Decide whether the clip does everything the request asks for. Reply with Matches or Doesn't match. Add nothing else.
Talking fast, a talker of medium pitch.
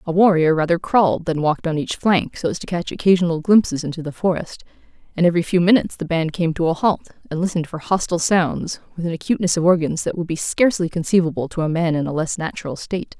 Matches